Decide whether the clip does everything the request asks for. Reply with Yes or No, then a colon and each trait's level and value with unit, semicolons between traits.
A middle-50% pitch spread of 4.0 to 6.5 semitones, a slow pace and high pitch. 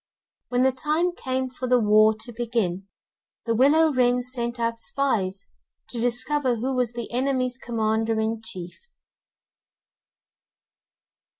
No: narrow, 2.5 semitones; slow, 125 wpm; high, 240 Hz